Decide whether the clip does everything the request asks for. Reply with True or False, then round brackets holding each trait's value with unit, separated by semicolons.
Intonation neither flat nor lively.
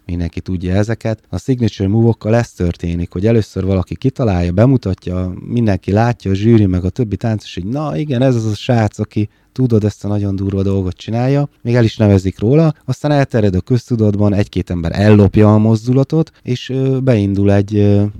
True (4.0 semitones)